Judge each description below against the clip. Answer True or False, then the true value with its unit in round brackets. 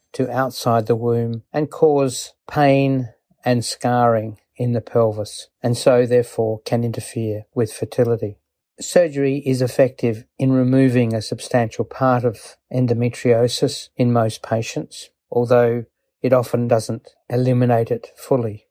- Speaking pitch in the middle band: False (120 Hz)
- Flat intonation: True (1.9 semitones)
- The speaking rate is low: True (125 wpm)